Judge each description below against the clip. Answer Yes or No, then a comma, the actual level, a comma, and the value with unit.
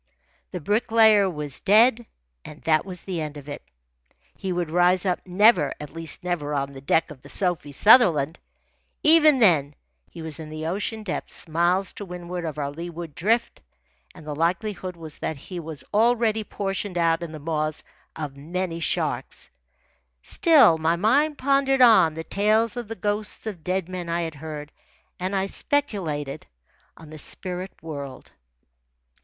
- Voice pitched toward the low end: No, medium, 175 Hz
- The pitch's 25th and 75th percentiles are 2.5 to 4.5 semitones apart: No, average, 5.0 semitones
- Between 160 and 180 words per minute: Yes, average, 165 wpm